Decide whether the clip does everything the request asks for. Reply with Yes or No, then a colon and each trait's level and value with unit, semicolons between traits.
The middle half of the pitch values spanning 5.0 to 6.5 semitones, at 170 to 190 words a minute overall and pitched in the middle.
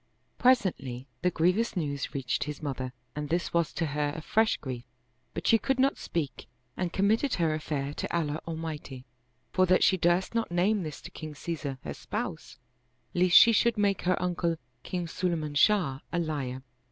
No: average, 4.1 semitones; average, 175 wpm; medium, 170 Hz